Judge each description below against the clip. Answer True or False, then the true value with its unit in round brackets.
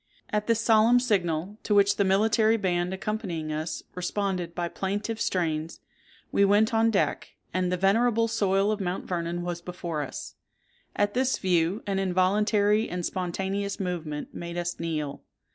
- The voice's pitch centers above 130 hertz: True (190 Hz)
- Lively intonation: False (3.3 semitones)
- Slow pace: False (155 wpm)